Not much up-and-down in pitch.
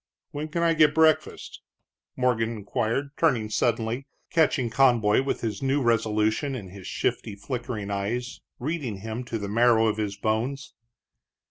No: average, 4.0 semitones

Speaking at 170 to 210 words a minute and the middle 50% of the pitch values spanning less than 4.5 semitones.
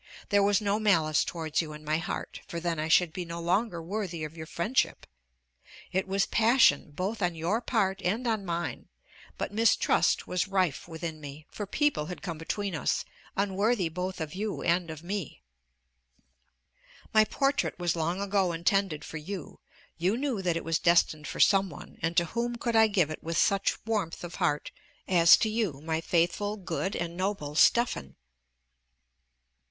Yes: average, 175 wpm; average, 3.8 semitones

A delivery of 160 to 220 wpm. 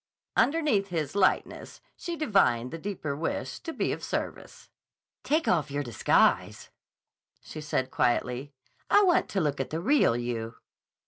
No: average, 145 wpm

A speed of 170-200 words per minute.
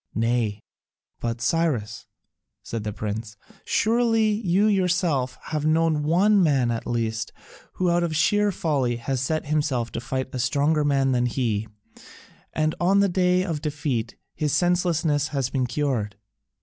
No: average, 150 wpm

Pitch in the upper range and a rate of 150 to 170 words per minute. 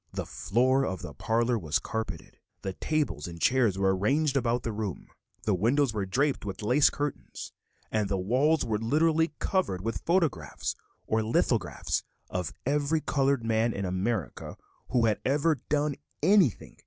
No: low, 115 Hz; average, 155 wpm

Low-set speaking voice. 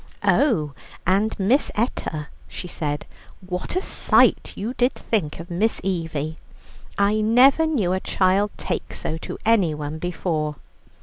No: medium, 185 Hz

